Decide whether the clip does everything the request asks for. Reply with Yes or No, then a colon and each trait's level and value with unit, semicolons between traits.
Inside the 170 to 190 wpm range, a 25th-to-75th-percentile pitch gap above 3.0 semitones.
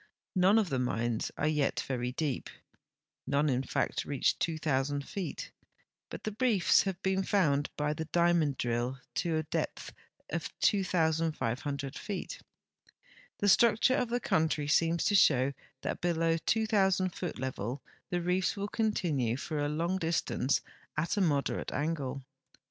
No: average, 150 wpm; average, 5.0 semitones